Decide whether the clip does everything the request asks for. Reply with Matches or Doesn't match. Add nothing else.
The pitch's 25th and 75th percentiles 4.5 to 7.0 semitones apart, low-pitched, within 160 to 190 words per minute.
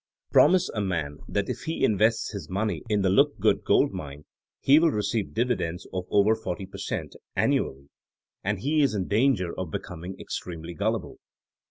Doesn't match